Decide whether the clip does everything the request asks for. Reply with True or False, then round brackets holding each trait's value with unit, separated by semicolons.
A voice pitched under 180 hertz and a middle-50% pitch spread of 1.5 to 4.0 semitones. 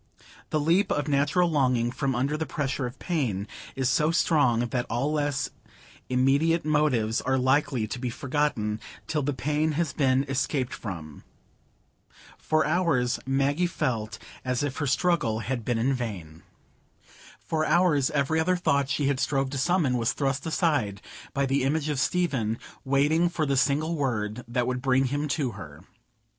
True (140 Hz; 3.5 semitones)